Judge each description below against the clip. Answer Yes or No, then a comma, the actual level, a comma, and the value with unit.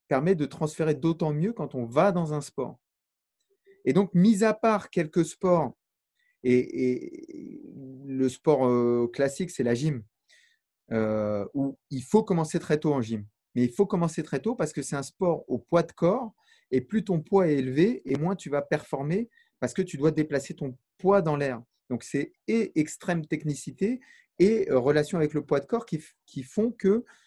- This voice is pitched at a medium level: Yes, medium, 160 Hz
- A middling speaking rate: Yes, average, 190 wpm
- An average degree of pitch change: No, wide, 6.4 semitones